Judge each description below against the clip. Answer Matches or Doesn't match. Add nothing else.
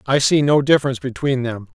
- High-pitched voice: Doesn't match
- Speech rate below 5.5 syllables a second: Doesn't match